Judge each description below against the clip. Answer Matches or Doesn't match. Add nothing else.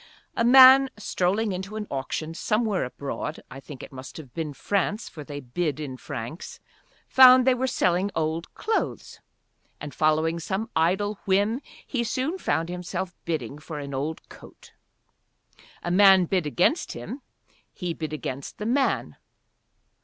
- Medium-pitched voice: Matches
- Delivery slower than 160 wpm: Matches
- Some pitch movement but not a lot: Doesn't match